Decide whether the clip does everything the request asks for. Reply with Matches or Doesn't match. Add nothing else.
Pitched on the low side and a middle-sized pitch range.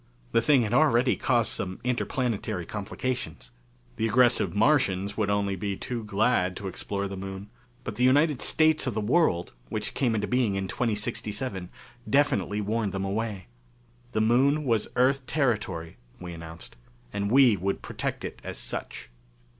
Matches